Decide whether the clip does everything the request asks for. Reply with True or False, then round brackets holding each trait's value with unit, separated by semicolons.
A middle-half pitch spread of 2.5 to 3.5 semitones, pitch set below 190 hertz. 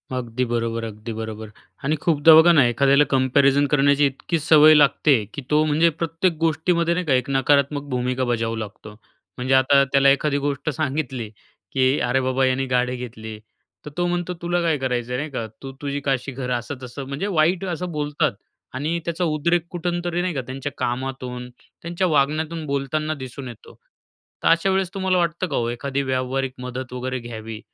False (3.9 semitones; 140 Hz)